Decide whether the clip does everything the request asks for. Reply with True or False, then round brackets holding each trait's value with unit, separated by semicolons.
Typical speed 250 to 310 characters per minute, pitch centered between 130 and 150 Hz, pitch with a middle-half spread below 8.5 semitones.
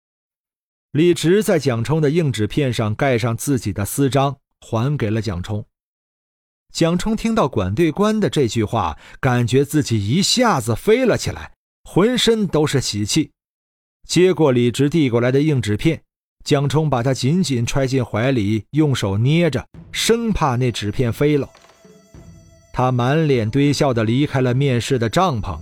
False (225 characters per minute; 135 Hz; 5.4 semitones)